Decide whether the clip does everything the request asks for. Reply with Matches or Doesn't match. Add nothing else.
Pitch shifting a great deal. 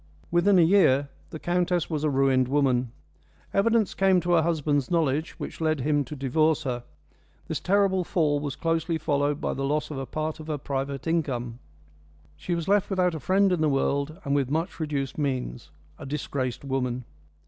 Doesn't match